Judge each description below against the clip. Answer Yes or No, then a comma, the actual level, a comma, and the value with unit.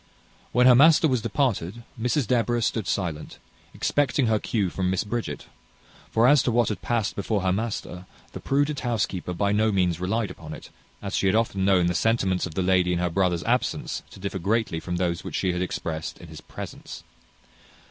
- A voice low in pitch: Yes, low, 100 Hz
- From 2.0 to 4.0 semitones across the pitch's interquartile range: No, average, 4.6 semitones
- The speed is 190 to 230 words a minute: Yes, average, 200 wpm